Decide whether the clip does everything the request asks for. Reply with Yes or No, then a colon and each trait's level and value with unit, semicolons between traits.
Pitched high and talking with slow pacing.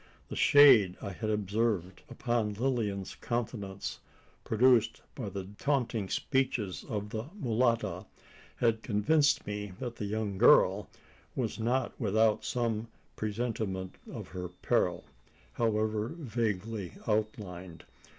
No: low, 110 Hz; slow, 110 wpm